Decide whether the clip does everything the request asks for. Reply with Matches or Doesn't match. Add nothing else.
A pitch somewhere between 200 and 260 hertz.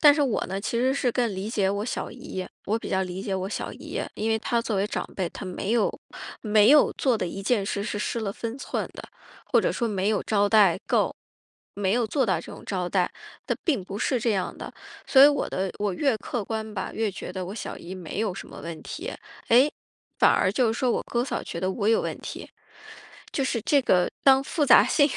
Matches